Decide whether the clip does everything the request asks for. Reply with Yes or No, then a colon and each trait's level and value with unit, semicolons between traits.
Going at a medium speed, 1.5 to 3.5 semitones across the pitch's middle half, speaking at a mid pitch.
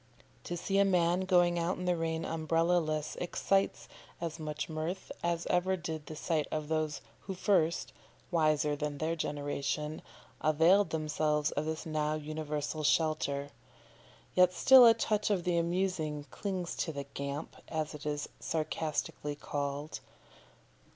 Yes: average, 145 wpm; narrow, 2.6 semitones; medium, 160 Hz